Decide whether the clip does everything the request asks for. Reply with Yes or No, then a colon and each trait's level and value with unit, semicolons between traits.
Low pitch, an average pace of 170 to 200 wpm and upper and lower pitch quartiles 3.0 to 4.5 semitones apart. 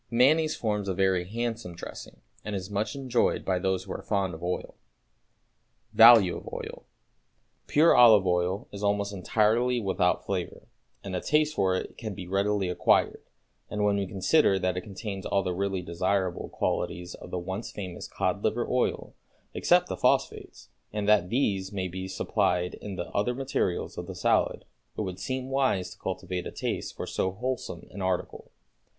Yes: low, 100 Hz; average, 180 wpm; average, 3.3 semitones